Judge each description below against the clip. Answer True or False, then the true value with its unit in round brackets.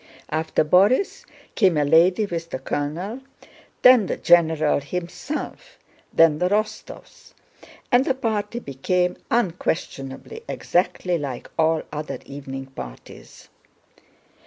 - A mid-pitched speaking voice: True (175 Hz)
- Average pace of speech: False (110 wpm)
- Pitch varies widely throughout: True (5.9 semitones)